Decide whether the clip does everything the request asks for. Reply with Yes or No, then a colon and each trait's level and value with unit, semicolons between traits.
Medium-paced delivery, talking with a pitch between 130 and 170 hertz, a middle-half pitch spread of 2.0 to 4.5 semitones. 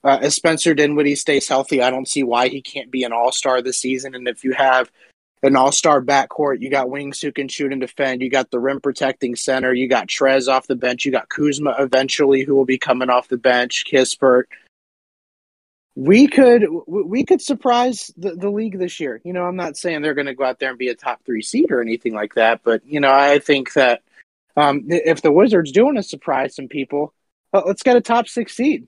No: fast, 225 wpm; medium, 140 Hz; average, 3.9 semitones